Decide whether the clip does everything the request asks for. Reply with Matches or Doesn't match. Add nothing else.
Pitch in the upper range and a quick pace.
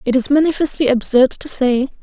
Doesn't match